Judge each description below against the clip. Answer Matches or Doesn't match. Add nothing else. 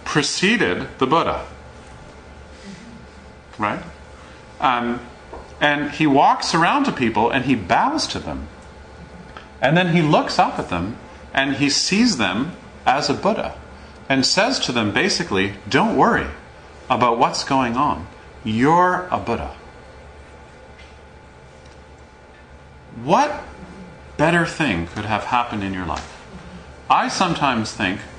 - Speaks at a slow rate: Matches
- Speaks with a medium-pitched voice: Doesn't match